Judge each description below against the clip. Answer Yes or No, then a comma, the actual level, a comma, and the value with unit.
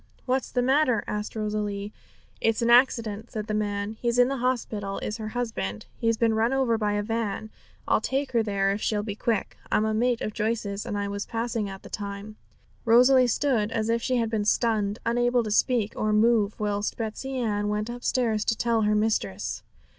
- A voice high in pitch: Yes, high, 220 Hz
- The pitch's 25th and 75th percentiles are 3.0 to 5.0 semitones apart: No, narrow, 2.4 semitones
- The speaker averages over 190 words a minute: Yes, average, 200 wpm